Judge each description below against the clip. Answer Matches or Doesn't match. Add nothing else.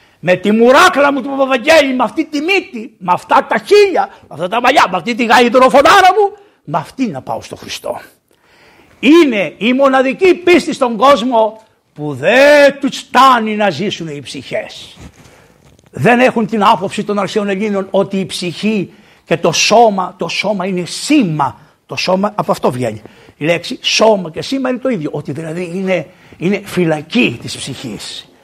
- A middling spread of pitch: Doesn't match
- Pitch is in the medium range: Doesn't match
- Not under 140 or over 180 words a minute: Matches